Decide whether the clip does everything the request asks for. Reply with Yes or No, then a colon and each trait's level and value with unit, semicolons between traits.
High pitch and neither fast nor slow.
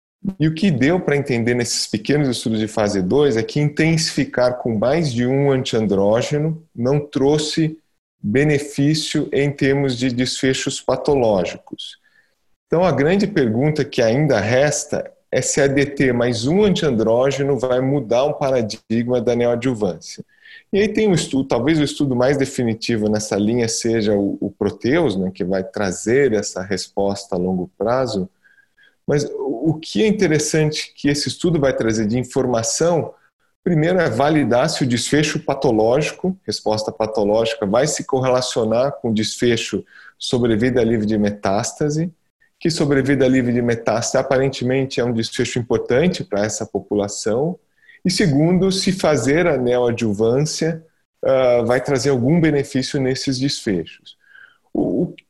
No: low, 135 Hz; average, 140 wpm